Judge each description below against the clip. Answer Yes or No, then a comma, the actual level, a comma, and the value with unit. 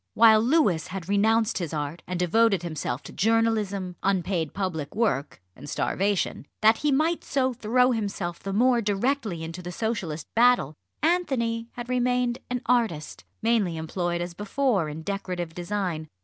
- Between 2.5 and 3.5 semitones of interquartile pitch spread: No, average, 5.3 semitones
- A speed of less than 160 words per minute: Yes, average, 150 wpm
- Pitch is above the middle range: Yes, high, 200 Hz